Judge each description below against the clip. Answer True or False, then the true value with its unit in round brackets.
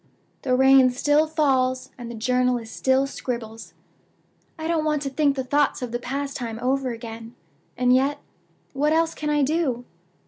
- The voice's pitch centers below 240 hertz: False (265 Hz)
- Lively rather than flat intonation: False (2.9 semitones)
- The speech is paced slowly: False (170 wpm)